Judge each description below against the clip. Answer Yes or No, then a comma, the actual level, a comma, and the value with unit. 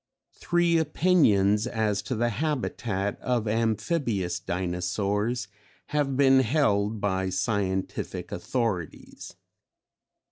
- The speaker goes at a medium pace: No, slow, 85 wpm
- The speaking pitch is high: No, low, 110 Hz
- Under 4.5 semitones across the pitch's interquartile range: No, average, 5.1 semitones